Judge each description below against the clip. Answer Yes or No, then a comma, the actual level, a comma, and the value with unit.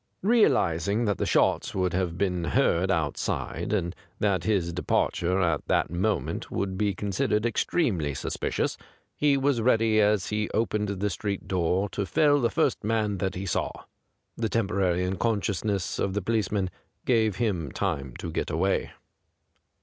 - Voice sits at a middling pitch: No, low, 100 Hz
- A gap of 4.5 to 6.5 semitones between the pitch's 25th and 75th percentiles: No, average, 3.2 semitones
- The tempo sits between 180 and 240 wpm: No, average, 160 wpm